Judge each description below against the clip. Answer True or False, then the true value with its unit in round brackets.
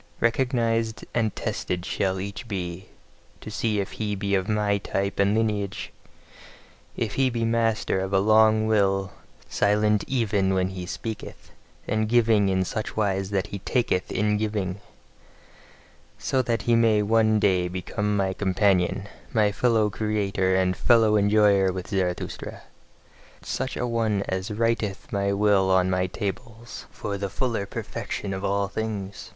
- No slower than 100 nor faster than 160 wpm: True (150 wpm)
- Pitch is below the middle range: True (105 Hz)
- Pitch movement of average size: False (2.3 semitones)